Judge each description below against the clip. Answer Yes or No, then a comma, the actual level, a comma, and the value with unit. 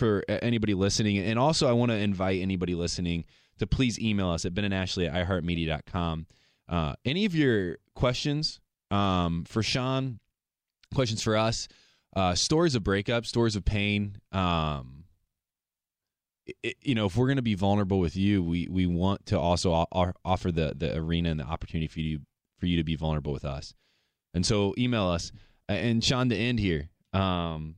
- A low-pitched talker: Yes, very low, 95 Hz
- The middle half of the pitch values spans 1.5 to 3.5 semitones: No, average, 4.7 semitones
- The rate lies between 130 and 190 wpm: Yes, average, 175 wpm